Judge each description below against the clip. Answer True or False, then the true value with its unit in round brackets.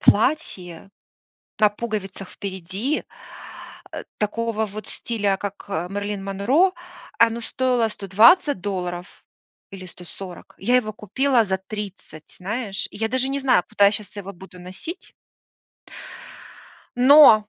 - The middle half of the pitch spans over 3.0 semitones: True (3.5 semitones)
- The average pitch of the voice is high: True (205 Hz)